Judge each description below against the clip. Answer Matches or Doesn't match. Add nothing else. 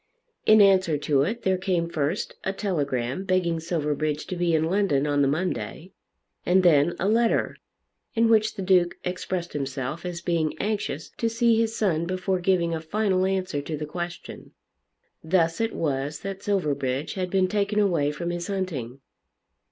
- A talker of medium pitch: Matches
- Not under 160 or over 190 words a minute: Matches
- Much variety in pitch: Doesn't match